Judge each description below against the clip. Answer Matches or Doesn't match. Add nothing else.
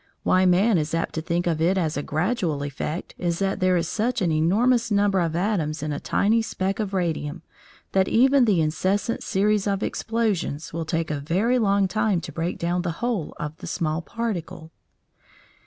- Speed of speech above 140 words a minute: Matches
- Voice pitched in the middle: Matches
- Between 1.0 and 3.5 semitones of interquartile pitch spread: Doesn't match